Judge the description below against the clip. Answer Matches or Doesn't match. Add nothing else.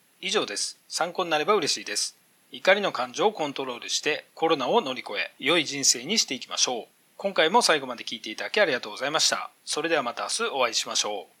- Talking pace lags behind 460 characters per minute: Doesn't match